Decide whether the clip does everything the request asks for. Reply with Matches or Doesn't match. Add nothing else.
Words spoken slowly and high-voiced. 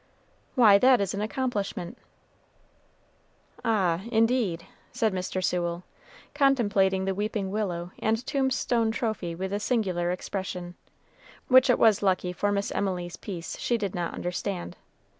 Matches